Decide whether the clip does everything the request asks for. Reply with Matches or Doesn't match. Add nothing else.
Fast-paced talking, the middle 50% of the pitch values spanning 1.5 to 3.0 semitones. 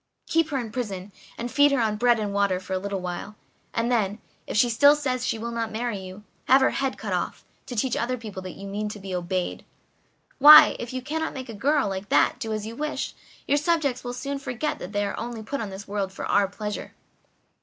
Doesn't match